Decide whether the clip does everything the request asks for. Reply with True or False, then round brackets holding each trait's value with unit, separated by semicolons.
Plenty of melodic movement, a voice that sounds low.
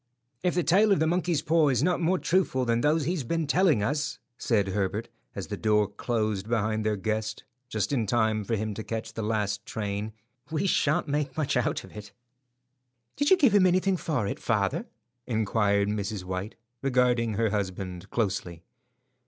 True (6.7 semitones; 115 Hz)